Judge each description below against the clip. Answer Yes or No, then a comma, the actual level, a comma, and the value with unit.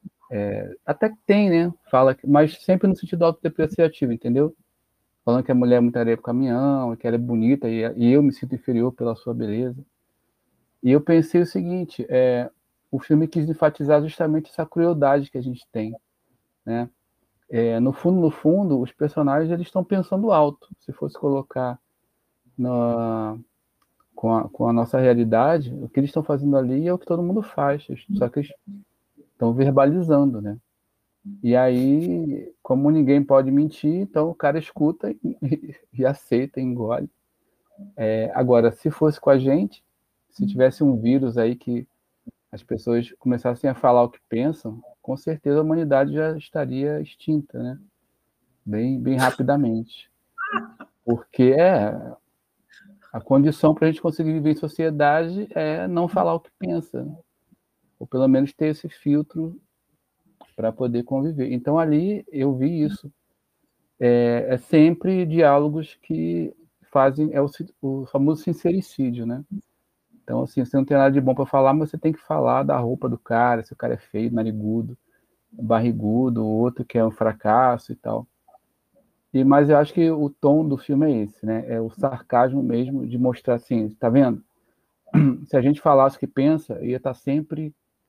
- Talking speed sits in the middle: Yes, average, 165 wpm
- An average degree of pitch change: Yes, average, 4.4 semitones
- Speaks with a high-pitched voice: No, low, 135 Hz